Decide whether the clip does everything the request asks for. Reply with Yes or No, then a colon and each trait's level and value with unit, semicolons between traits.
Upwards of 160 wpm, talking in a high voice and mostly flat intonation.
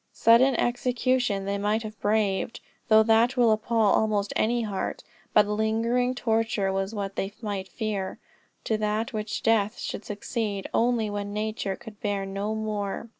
No: average, 150 wpm; high, 215 Hz; narrow, 1.9 semitones